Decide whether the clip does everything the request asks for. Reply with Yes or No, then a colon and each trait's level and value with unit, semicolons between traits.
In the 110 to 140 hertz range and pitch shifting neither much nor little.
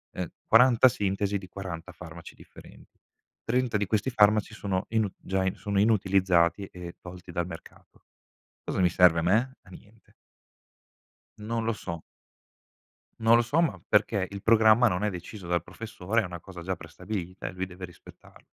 No: low, 100 Hz; average, 3.6 semitones